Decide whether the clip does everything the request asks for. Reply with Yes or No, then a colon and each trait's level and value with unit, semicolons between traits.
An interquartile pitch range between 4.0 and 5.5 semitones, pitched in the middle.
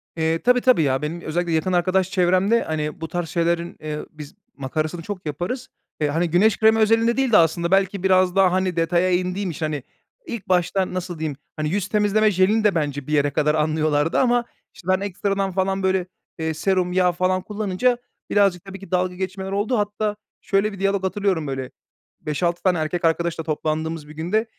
No: average, 3.6 semitones; medium, 180 Hz